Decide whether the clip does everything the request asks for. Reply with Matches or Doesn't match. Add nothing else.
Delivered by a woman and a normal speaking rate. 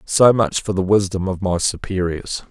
Doesn't match